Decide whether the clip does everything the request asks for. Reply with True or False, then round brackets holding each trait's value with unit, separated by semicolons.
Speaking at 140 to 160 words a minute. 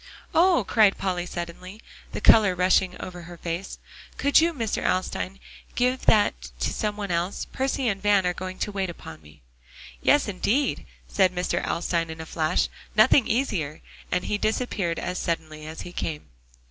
False (170 wpm)